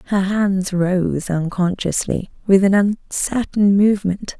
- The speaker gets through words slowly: Yes, slow, 110 wpm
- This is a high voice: Yes, high, 195 Hz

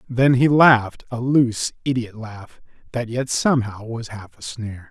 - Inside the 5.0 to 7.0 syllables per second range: No, 4.5 syllables/s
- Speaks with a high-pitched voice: No, low, 120 Hz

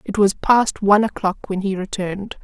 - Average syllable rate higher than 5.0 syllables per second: Yes, 5.2 syllables/s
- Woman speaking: Yes, female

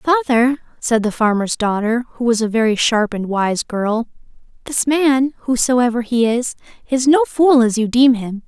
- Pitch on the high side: Yes, high, 240 Hz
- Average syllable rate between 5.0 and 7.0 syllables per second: No, 4.4 syllables/s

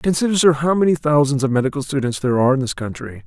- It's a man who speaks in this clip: Yes, male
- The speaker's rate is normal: No, fast, 240 wpm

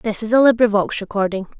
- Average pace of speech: Yes, average, 190 wpm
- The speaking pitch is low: No, high, 215 Hz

